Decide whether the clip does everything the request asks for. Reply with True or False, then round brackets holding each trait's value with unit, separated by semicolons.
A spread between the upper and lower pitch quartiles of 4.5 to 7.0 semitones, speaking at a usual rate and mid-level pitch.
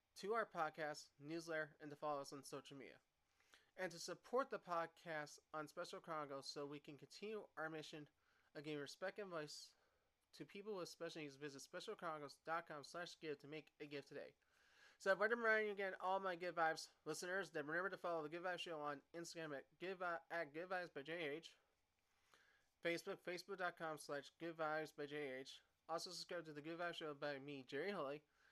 False (3.3 semitones; 185 wpm; 160 Hz)